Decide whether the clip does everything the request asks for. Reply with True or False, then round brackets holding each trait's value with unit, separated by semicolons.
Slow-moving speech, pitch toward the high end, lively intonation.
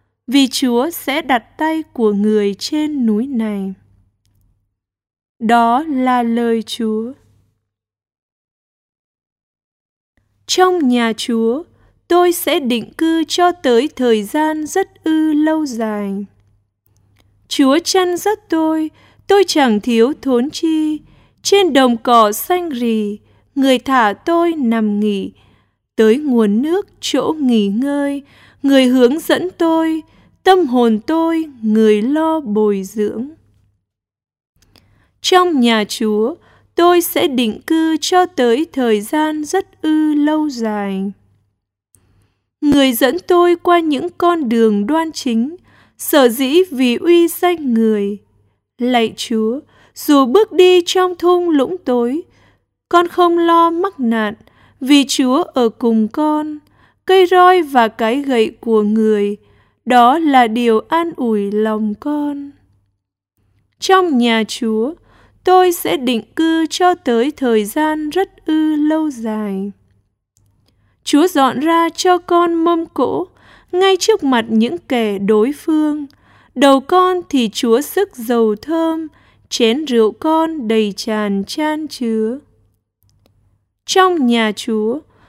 True (120 wpm; 255 Hz; 6.9 semitones)